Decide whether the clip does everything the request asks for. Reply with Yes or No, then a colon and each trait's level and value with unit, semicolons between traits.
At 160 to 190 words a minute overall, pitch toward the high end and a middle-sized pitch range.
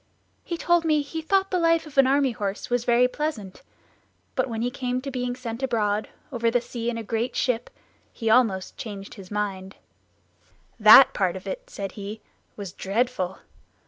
Yes: average, 180 wpm; high, 240 Hz; average, 4.5 semitones